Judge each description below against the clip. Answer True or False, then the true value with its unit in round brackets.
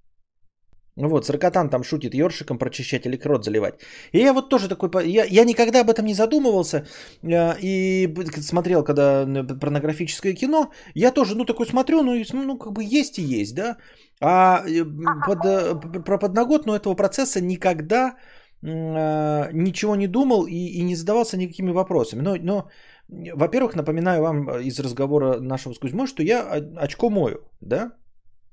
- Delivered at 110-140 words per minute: False (150 wpm)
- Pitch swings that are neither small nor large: False (6.9 semitones)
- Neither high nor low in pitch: True (180 Hz)